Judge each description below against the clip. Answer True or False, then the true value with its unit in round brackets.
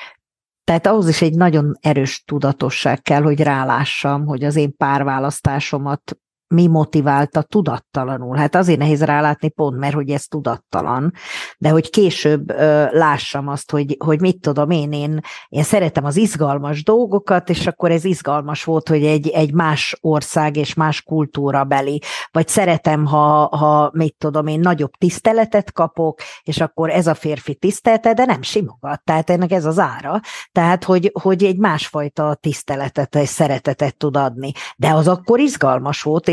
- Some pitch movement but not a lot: True (3.0 semitones)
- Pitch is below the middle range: False (155 Hz)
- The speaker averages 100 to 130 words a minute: False (155 wpm)